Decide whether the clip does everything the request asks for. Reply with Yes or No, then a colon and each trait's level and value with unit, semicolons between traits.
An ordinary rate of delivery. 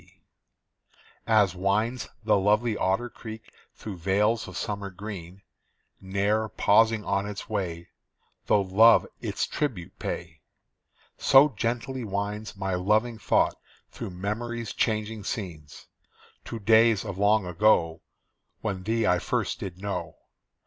No: slow, 125 wpm